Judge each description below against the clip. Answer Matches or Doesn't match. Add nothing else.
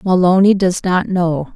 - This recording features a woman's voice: Matches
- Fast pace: Doesn't match